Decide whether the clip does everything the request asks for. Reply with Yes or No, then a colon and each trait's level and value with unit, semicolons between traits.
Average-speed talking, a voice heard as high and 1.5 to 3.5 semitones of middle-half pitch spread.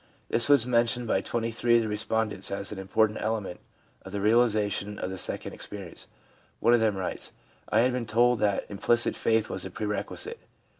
No: average, 195 wpm; low, 110 Hz; narrow, 2.5 semitones